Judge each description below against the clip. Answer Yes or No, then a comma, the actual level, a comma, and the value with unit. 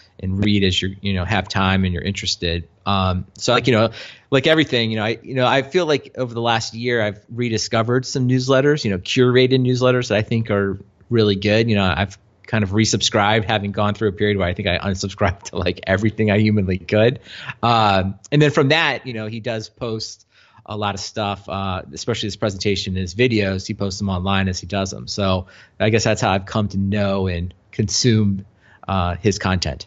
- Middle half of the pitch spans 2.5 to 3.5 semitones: Yes, average, 3.1 semitones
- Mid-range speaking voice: No, low, 105 Hz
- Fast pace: Yes, fast, 220 wpm